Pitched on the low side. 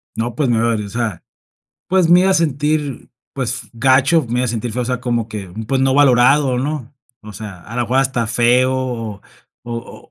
Yes: low, 125 Hz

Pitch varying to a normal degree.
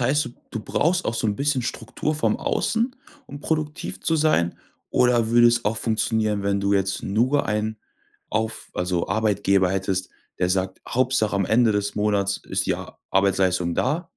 Yes: average, 4.2 semitones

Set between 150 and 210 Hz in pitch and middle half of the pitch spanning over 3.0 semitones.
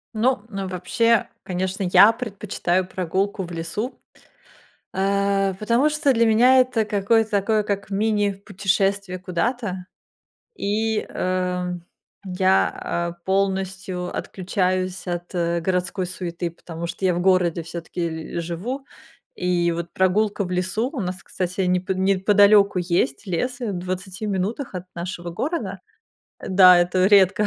No: high, 190 Hz; narrow, 2.5 semitones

